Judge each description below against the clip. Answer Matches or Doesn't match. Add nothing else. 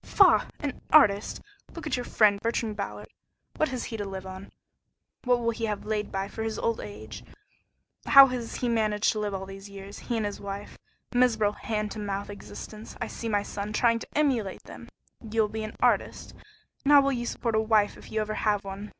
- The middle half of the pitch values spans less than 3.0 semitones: Matches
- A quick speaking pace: Matches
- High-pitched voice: Matches